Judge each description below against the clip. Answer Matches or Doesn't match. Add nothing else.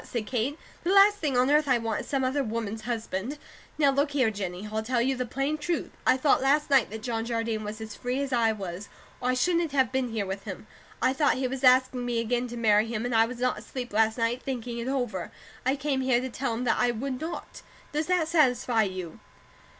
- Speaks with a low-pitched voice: Doesn't match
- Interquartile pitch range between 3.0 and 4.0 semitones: Matches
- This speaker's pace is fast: Matches